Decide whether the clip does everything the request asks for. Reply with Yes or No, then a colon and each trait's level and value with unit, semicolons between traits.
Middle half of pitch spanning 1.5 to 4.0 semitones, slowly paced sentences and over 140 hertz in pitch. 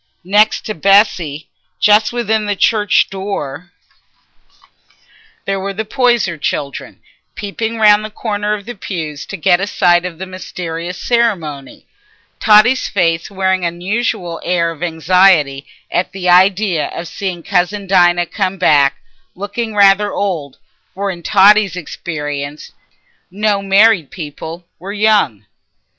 Yes: average, 3.6 semitones; slow, 130 wpm; high, 190 Hz